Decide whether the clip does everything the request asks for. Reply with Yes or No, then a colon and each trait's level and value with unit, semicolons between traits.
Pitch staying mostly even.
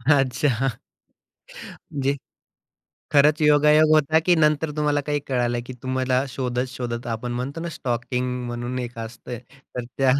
No: average, 3.2 semitones